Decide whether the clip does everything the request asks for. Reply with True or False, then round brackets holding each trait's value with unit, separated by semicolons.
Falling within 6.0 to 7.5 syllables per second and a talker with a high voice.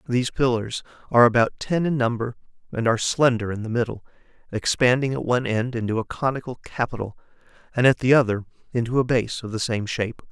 False (6.4 syllables/s; 120 Hz)